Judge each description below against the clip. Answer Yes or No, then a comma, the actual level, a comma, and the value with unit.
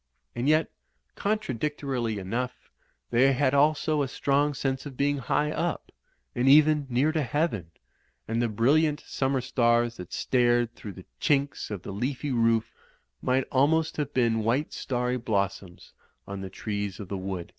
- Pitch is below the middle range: Yes, low, 125 Hz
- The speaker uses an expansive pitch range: No, average, 4.2 semitones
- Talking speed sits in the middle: Yes, average, 155 wpm